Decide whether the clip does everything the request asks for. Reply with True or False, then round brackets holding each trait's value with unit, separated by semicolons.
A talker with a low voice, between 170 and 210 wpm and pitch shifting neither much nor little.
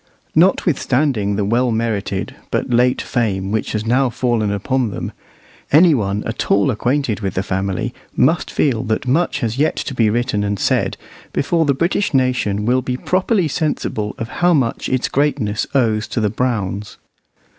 True (120 Hz; 175 wpm; 4.6 semitones)